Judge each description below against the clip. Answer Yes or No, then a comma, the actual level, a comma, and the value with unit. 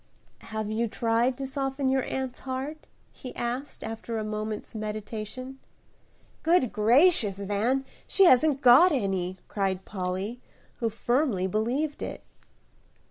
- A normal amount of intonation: Yes, average, 3.9 semitones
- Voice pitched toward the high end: Yes, high, 235 Hz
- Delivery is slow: Yes, slow, 125 wpm